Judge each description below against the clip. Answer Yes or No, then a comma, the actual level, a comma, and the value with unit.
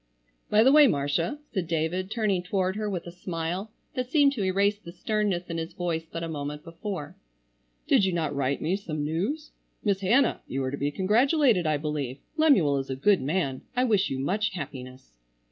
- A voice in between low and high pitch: Yes, medium, 180 Hz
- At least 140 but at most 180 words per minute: No, average, 195 wpm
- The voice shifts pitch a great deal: Yes, wide, 5.7 semitones